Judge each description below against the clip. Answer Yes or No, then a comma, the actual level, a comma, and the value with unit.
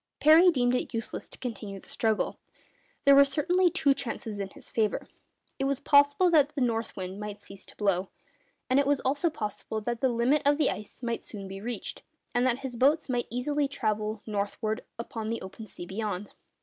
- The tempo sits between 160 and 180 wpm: No, average, 200 wpm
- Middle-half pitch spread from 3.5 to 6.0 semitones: Yes, average, 4.9 semitones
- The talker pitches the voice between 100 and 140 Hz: No, high, 235 Hz